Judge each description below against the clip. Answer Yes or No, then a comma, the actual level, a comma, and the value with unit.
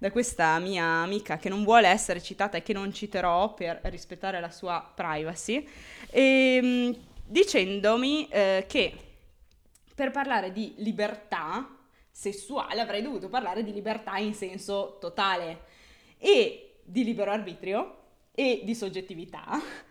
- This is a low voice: No, high, 205 Hz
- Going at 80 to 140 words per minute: Yes, average, 125 wpm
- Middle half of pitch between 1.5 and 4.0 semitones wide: No, average, 4.6 semitones